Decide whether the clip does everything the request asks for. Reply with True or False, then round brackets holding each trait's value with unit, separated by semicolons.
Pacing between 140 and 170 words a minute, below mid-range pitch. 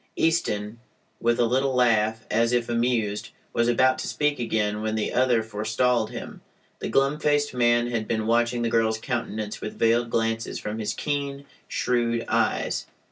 True (165 wpm; 115 Hz)